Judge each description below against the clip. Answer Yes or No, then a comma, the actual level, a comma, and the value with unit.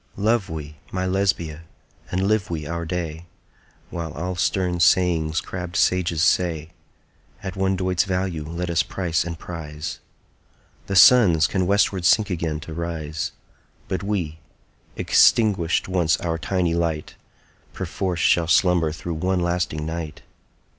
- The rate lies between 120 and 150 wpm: Yes, average, 140 wpm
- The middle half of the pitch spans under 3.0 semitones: Yes, narrow, 2.4 semitones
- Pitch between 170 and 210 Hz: No, very low, 85 Hz